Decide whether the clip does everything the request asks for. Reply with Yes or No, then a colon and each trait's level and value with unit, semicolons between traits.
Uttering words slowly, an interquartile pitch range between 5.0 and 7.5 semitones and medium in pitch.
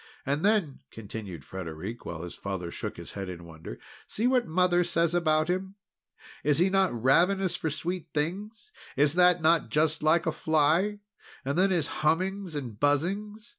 No: average, 170 wpm; wide, 5.6 semitones; medium, 160 Hz